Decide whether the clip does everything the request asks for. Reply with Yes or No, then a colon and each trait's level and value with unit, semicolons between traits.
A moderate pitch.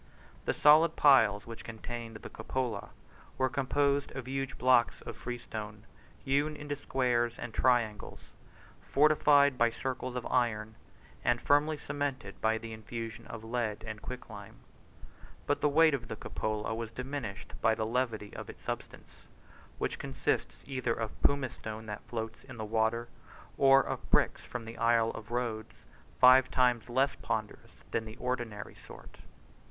No: low, 120 Hz